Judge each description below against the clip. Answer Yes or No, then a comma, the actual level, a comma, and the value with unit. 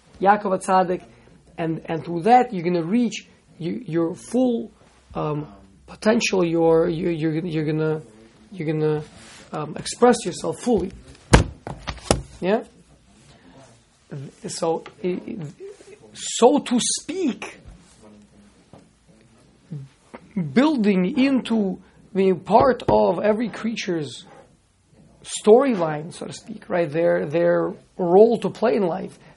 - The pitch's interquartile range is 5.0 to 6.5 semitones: Yes, average, 5.3 semitones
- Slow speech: Yes, slow, 105 wpm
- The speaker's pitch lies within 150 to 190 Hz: Yes, medium, 185 Hz